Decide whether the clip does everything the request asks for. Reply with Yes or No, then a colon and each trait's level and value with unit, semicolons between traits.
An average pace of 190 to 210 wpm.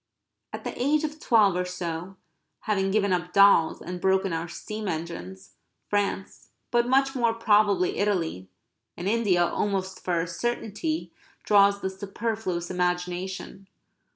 No: slow, 135 wpm